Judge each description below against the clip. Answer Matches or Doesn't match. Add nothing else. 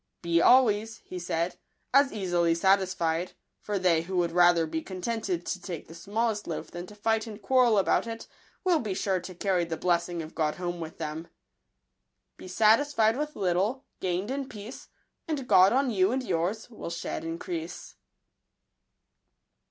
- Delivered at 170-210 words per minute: Matches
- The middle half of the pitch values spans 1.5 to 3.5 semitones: Doesn't match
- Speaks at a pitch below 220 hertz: Matches